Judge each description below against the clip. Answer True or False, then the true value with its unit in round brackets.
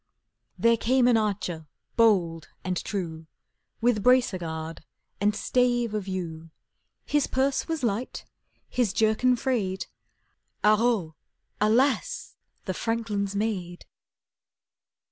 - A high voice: True (215 Hz)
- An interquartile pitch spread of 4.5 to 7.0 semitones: True (4.8 semitones)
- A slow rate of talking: True (105 wpm)